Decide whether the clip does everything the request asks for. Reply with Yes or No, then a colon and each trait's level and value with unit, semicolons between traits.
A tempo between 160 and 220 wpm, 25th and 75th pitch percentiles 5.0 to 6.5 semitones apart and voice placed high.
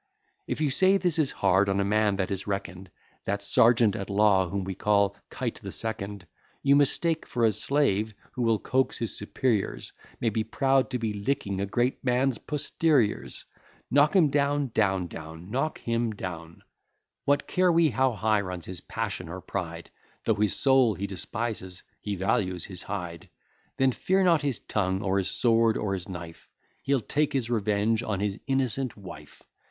No: average, 170 wpm; average, 5.3 semitones; low, 110 Hz